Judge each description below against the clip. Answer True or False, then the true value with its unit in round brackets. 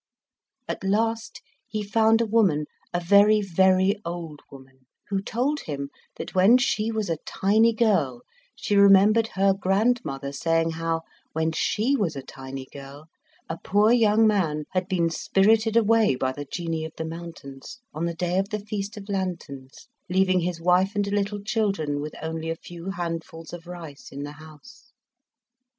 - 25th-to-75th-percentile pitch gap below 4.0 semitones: False (4.6 semitones)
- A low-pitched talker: False (185 Hz)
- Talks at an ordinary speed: True (165 wpm)